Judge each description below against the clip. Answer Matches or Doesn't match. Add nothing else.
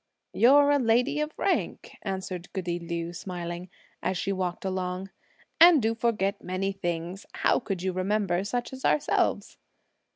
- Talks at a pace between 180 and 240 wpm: Doesn't match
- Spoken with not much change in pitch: Doesn't match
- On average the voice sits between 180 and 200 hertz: Matches